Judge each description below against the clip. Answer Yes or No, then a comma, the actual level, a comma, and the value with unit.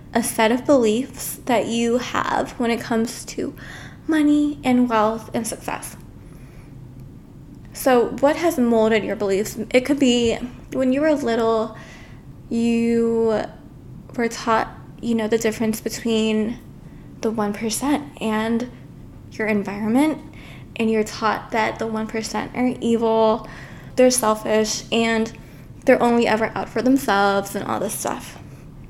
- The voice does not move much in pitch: Yes, narrow, 2.1 semitones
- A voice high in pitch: Yes, high, 230 Hz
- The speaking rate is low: Yes, slow, 130 wpm